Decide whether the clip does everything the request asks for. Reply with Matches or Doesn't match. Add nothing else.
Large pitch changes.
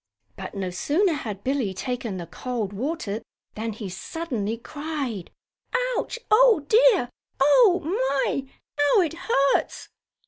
Matches